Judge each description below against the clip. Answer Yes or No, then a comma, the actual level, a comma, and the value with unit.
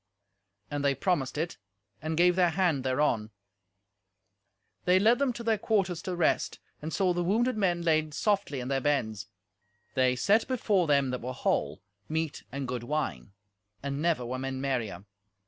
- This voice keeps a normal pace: Yes, average, 165 wpm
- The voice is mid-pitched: Yes, medium, 155 Hz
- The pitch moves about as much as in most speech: No, wide, 5.8 semitones